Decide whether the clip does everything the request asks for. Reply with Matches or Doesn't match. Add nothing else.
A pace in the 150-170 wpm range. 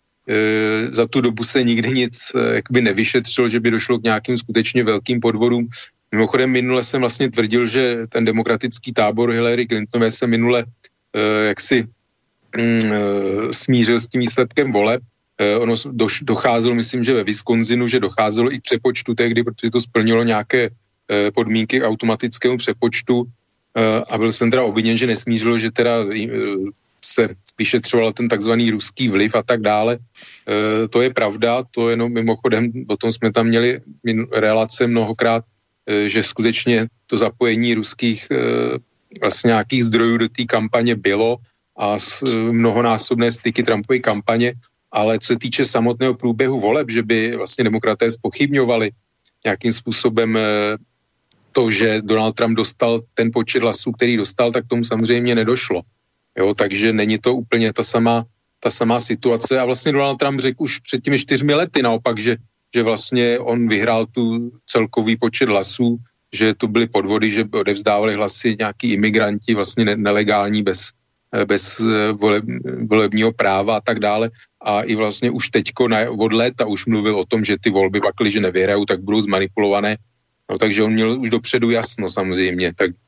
Matches